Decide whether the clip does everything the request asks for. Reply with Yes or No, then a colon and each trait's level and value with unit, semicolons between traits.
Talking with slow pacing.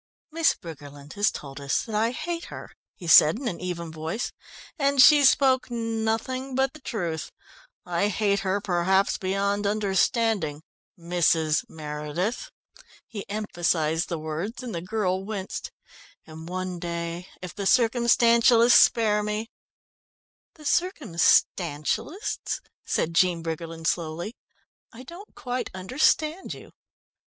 Yes: slow, 125 wpm